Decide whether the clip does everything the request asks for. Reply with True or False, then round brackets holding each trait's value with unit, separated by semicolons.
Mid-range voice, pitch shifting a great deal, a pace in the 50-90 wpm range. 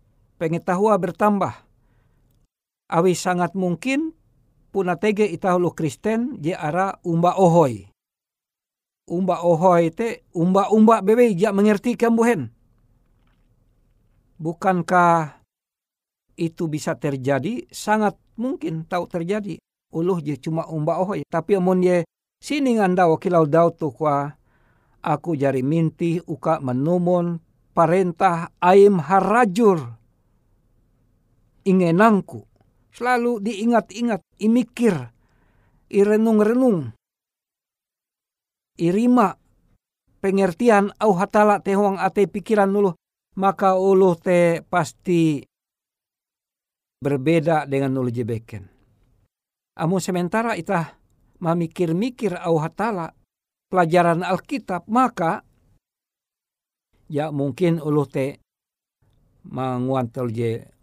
True (170 Hz; 6.3 semitones; 85 wpm)